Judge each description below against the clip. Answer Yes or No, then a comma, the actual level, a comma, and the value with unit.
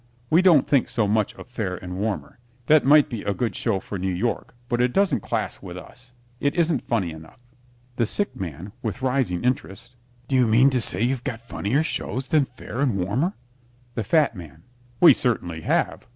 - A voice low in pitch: Yes, low, 120 Hz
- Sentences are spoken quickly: No, average, 195 wpm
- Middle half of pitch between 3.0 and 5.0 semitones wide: No, wide, 5.5 semitones